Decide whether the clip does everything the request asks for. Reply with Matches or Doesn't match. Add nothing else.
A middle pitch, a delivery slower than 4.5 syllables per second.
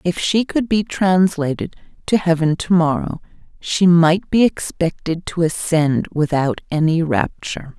Matches